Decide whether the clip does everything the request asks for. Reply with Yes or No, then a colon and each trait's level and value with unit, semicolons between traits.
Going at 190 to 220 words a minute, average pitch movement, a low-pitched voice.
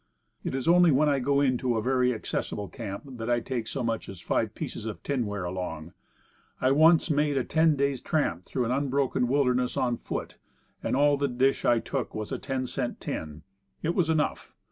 Yes: average, 200 wpm; average, 3.7 semitones; low, 130 Hz